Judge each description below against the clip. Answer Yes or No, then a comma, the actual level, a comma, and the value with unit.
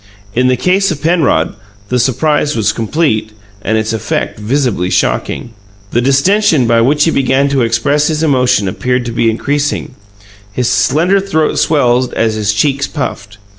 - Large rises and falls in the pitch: No, average, 4.7 semitones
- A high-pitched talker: No, low, 130 Hz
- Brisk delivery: No, average, 160 wpm